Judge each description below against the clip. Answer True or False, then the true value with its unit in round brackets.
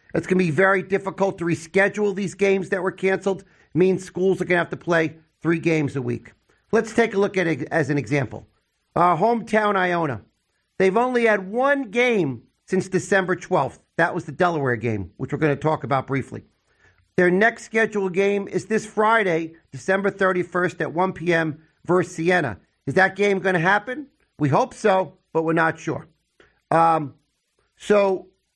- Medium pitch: True (180 Hz)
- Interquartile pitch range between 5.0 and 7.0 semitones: False (3.8 semitones)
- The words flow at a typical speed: True (185 wpm)